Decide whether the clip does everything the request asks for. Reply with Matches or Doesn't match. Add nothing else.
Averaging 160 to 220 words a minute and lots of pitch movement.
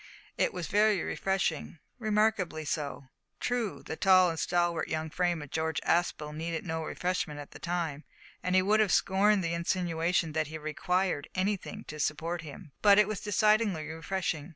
Doesn't match